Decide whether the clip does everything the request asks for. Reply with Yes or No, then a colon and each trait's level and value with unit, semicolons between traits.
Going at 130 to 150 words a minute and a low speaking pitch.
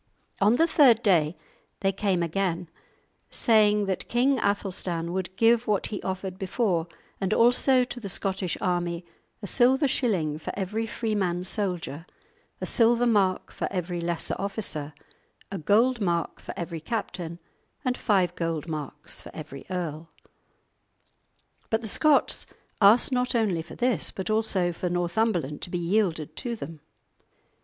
No: average, 145 wpm; high, 190 Hz